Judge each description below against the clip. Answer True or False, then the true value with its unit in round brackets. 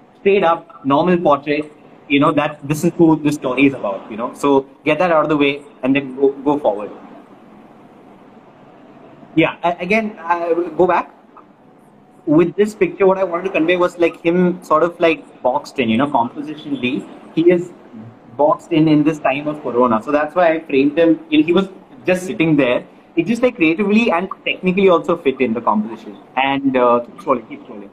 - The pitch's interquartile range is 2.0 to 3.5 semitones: False (3.9 semitones)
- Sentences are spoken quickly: False (195 wpm)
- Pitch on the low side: False (160 Hz)